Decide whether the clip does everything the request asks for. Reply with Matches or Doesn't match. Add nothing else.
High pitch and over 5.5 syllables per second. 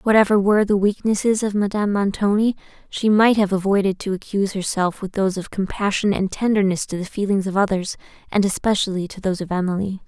Matches